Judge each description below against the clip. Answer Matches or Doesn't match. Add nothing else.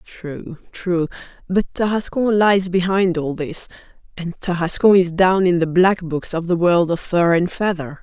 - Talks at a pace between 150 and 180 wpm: Matches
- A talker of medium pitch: Matches